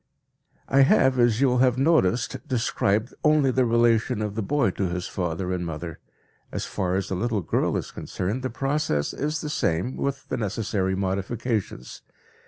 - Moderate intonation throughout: No, wide, 5.7 semitones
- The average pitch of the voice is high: No, low, 115 Hz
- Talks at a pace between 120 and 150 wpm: No, average, 175 wpm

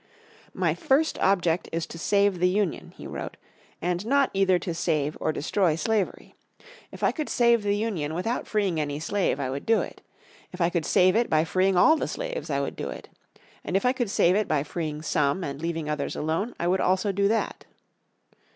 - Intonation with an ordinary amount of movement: Yes, average, 4.6 semitones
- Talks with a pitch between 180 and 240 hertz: Yes, medium, 185 Hz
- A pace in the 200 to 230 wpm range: Yes, fast, 205 wpm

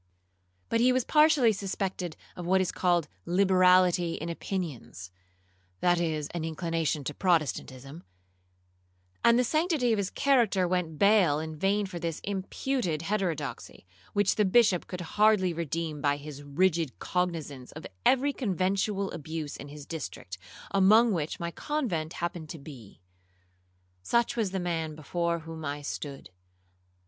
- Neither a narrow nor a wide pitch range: Yes, average, 4.1 semitones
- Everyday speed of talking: Yes, average, 145 wpm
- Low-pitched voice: No, medium, 175 Hz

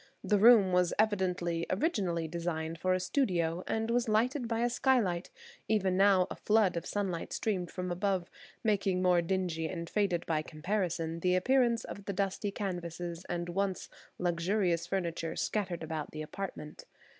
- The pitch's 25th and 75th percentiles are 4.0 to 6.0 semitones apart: No, average, 3.2 semitones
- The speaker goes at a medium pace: Yes, average, 155 wpm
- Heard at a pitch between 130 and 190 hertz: Yes, medium, 185 Hz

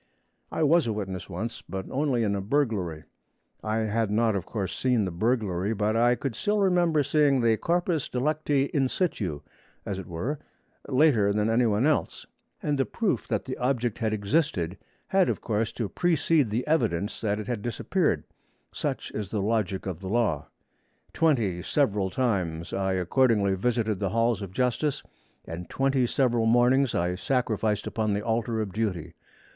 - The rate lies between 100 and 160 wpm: No, average, 170 wpm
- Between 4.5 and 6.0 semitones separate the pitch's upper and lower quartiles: Yes, average, 5.1 semitones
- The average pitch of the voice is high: No, low, 115 Hz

